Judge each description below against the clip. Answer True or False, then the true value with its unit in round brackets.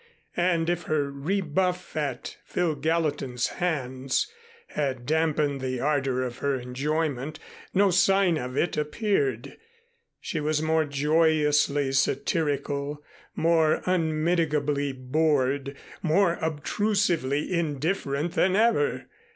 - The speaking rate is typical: False (100 wpm)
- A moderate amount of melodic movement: True (3.3 semitones)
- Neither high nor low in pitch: True (150 Hz)